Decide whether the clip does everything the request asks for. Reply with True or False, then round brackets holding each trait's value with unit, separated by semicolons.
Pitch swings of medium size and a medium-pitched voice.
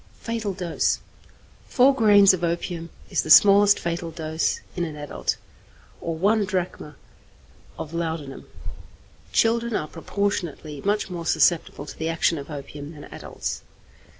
True (4.2 semitones; 170 Hz)